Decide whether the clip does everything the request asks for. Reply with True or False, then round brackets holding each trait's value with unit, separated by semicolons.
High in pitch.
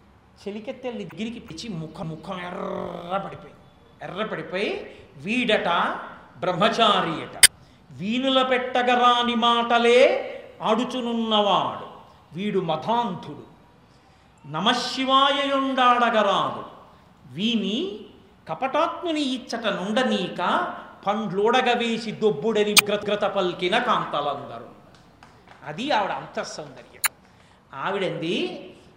True (215 Hz)